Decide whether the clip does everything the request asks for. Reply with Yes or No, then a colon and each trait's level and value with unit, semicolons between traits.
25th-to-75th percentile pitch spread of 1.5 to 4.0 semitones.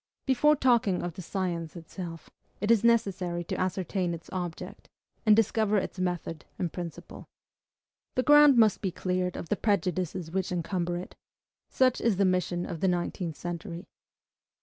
Yes: average, 3.1 semitones